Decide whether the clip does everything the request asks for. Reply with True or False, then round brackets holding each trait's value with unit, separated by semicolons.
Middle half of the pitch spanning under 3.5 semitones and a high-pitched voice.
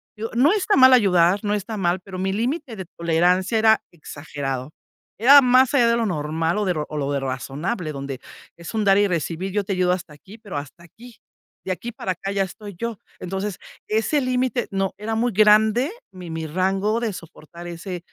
False (4.7 semitones; 195 Hz)